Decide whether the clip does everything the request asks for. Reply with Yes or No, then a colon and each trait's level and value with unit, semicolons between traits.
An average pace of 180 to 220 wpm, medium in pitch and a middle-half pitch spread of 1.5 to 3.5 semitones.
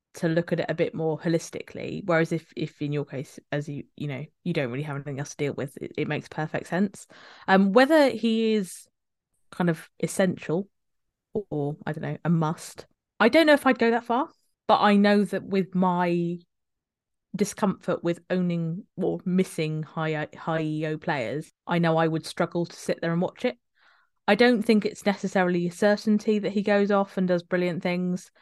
No: average, 200 wpm; medium, 175 Hz; average, 4.3 semitones